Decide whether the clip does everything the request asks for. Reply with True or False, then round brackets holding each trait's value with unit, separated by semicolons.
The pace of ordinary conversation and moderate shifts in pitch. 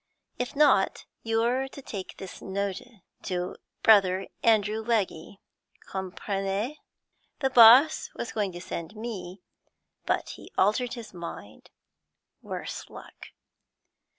False (110 wpm; 4.0 semitones)